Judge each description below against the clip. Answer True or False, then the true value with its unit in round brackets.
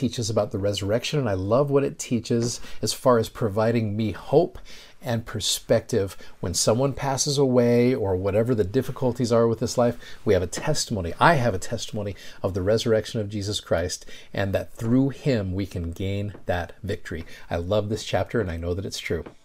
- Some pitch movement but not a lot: True (3.3 semitones)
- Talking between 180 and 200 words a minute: True (195 wpm)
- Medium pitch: False (115 Hz)